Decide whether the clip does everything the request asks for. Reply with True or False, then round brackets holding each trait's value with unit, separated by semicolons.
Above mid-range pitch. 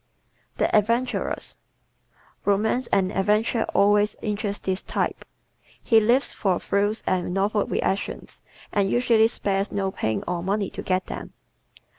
True (205 Hz)